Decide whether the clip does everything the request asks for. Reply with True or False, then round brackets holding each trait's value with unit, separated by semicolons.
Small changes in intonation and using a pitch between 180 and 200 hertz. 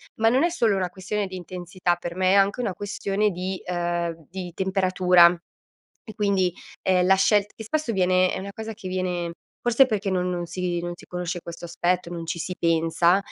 True (2.3 semitones; 185 Hz)